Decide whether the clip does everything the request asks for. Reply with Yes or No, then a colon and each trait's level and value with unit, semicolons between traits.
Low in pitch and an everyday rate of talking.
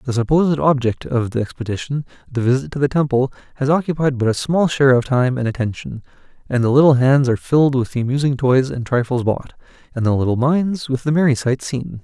No: low, 130 Hz; fast, 215 wpm